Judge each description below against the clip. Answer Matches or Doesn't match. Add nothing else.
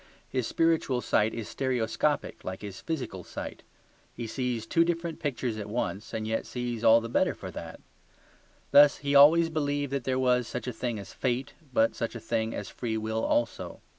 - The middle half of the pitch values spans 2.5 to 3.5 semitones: Doesn't match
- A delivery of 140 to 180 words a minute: Doesn't match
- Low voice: Matches